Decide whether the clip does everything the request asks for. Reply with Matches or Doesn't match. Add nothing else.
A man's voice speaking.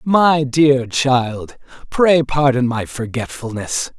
Matches